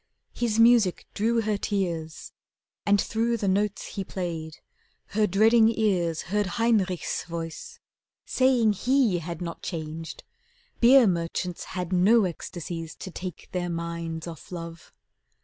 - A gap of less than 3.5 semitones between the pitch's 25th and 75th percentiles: No, average, 4.6 semitones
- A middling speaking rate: No, slow, 130 wpm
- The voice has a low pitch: No, medium, 185 Hz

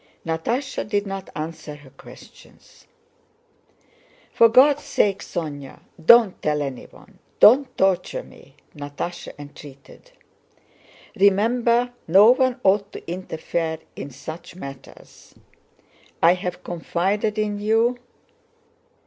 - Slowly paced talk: Yes, slow, 100 wpm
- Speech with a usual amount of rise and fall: No, wide, 6.0 semitones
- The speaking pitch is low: No, high, 190 Hz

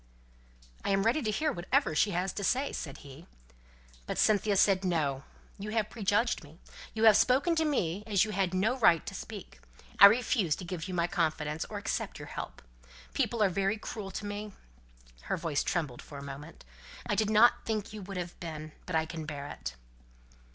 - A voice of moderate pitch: No, high, 195 Hz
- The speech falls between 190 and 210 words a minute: Yes, average, 200 wpm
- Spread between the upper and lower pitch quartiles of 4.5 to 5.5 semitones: Yes, average, 4.9 semitones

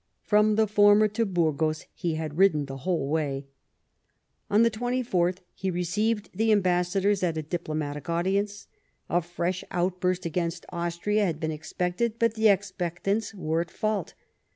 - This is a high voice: No, medium, 180 Hz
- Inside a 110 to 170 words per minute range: Yes, average, 150 wpm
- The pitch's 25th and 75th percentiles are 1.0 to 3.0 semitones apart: No, average, 3.7 semitones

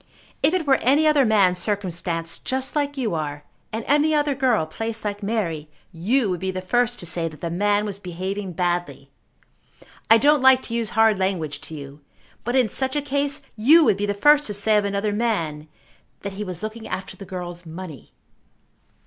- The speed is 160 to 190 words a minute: No, average, 200 wpm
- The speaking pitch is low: No, high, 205 Hz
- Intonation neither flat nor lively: No, wide, 6.2 semitones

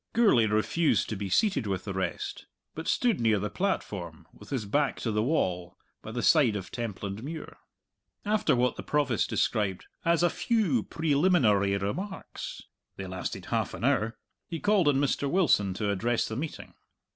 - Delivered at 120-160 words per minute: No, average, 170 wpm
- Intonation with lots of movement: Yes, wide, 8.1 semitones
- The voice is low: Yes, low, 120 Hz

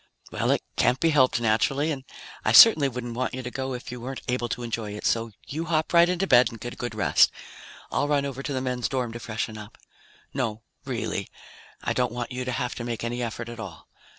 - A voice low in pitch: Yes, low, 125 Hz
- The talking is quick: Yes, fast, 235 wpm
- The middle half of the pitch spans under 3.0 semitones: Yes, narrow, 2.5 semitones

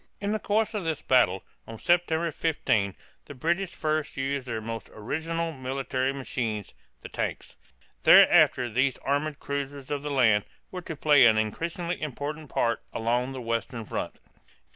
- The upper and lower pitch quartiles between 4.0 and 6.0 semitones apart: Yes, average, 5.2 semitones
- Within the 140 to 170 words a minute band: Yes, average, 155 wpm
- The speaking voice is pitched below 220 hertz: Yes, medium, 140 Hz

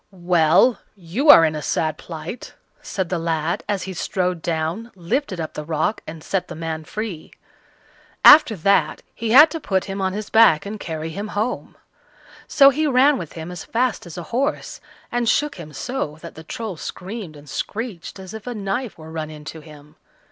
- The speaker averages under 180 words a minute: No, average, 190 wpm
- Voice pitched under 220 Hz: Yes, medium, 185 Hz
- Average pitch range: No, wide, 5.9 semitones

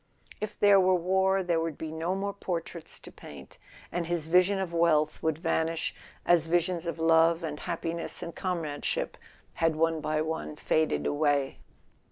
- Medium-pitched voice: Yes, medium, 165 Hz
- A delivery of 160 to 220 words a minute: Yes, average, 170 wpm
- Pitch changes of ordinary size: No, narrow, 2.1 semitones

